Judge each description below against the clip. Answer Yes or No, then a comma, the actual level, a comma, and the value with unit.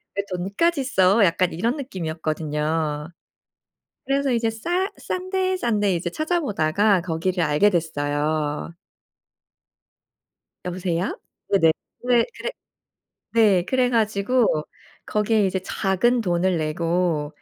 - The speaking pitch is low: No, high, 190 Hz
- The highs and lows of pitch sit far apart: Yes, wide, 6.1 semitones